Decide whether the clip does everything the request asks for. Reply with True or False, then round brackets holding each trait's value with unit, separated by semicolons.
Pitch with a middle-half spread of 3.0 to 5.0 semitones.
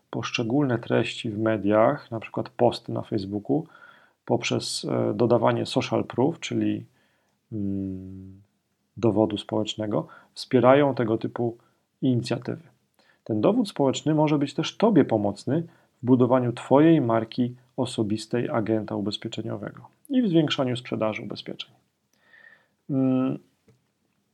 True (3.4 semitones)